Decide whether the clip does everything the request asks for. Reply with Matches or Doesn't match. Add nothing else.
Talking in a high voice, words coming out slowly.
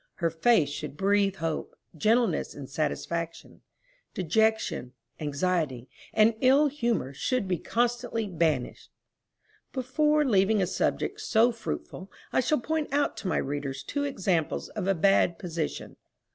Matches